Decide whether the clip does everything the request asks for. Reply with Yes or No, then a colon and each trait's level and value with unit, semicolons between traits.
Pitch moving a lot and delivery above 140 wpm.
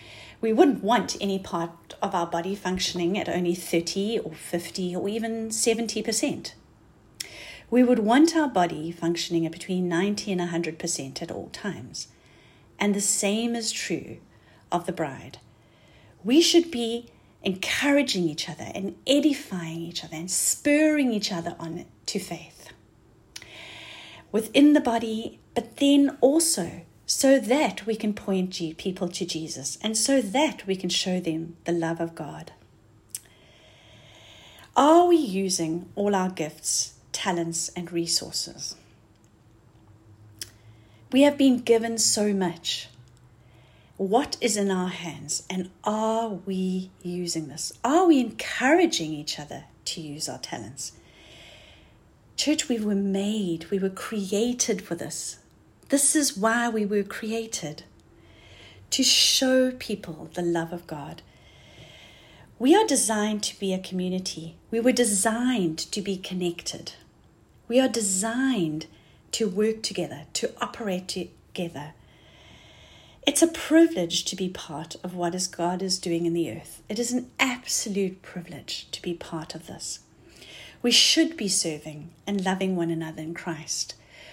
No: wide, 5.8 semitones; slow, 135 wpm